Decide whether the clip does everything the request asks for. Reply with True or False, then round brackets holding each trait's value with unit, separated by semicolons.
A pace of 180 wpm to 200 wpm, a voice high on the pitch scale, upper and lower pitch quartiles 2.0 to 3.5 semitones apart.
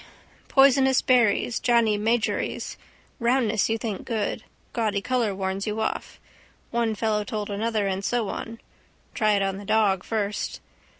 False (140 wpm; 220 Hz; 2.5 semitones)